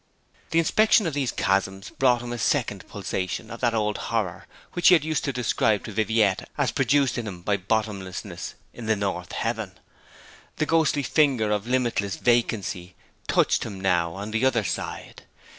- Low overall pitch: Yes, low, 110 Hz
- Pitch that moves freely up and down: No, average, 5.0 semitones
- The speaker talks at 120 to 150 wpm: No, average, 175 wpm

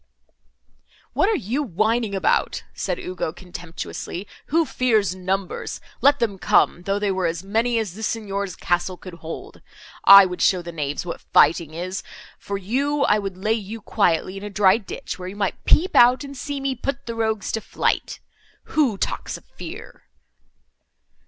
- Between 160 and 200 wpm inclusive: Yes, average, 165 wpm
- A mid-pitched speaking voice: No, high, 200 Hz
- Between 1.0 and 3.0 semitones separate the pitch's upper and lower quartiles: No, average, 4.2 semitones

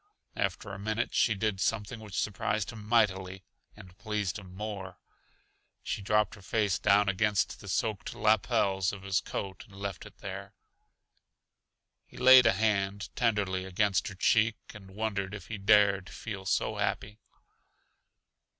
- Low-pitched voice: Yes, low, 100 Hz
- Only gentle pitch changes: Yes, narrow, 2.0 semitones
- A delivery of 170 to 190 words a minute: No, average, 150 wpm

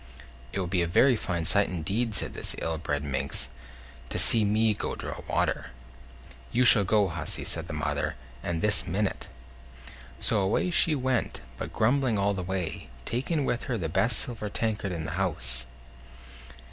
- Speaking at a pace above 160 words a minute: Yes, average, 170 wpm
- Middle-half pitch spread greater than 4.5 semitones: Yes, average, 4.9 semitones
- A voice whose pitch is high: No, low, 100 Hz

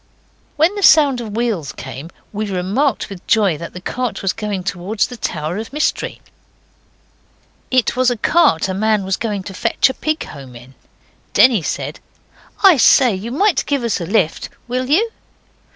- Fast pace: No, average, 175 wpm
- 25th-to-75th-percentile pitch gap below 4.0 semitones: No, wide, 5.6 semitones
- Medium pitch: No, high, 215 Hz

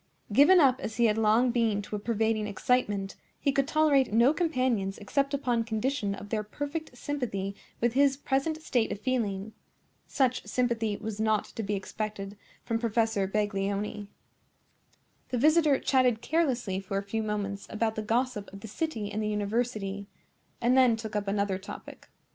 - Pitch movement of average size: Yes, average, 3.8 semitones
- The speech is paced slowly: No, average, 165 wpm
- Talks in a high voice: Yes, high, 225 Hz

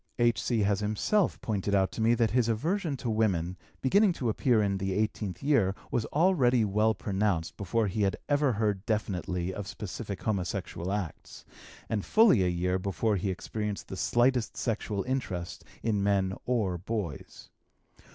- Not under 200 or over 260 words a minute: No, average, 160 wpm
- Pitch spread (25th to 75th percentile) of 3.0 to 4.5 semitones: Yes, average, 3.7 semitones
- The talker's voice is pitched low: Yes, low, 105 Hz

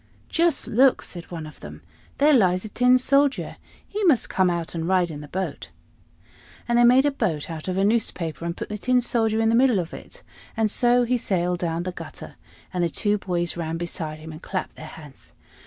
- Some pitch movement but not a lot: No, wide, 6.1 semitones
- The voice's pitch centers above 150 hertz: Yes, high, 190 Hz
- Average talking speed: No, fast, 220 wpm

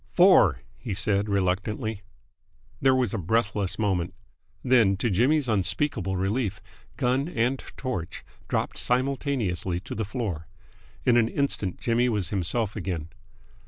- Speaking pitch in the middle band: No, low, 110 Hz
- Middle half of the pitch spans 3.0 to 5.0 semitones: Yes, average, 4.7 semitones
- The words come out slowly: Yes, slow, 125 wpm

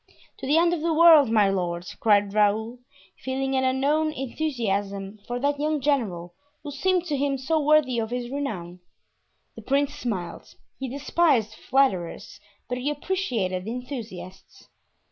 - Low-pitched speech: No, very high, 260 Hz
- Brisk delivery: No, average, 145 wpm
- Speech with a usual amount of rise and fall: No, wide, 5.8 semitones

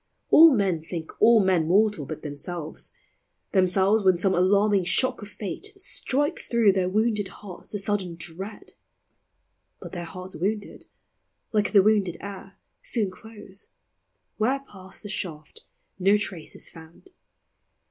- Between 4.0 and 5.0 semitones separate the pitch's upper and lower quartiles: No, average, 3.0 semitones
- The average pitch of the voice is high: Yes, high, 195 Hz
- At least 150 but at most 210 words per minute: No, slow, 135 wpm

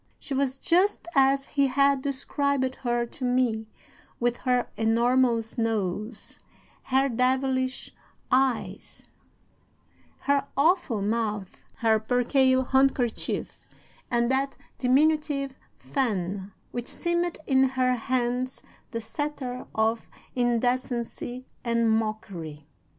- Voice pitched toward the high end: Yes, very high, 255 Hz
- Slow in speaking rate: Yes, slow, 100 wpm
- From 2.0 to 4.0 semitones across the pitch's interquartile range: Yes, average, 2.8 semitones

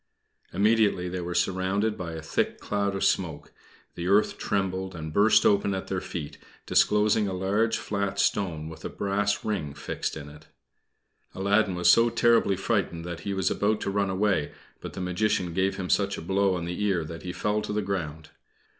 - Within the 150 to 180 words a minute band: No, average, 190 wpm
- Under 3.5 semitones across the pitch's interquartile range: Yes, average, 2.7 semitones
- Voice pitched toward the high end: No, very low, 95 Hz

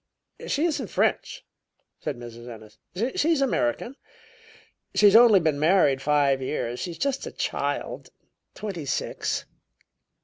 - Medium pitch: Yes, medium, 155 Hz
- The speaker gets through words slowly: Yes, slow, 125 wpm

